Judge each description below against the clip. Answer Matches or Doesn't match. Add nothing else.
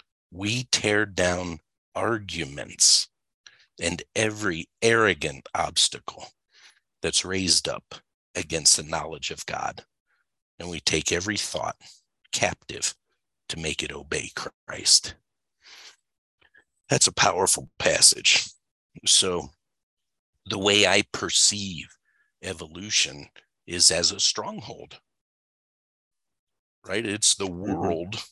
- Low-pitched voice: Matches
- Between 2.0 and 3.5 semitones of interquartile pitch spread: Matches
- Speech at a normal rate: Doesn't match